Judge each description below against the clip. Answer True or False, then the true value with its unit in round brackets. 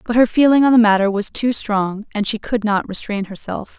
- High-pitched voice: True (215 Hz)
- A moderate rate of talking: False (240 wpm)